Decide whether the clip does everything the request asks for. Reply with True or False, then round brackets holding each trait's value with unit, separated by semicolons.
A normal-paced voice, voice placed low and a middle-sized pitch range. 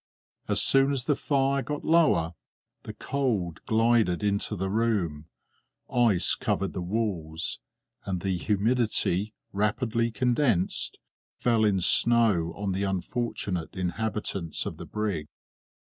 False (120 wpm; 105 Hz; 4.4 semitones)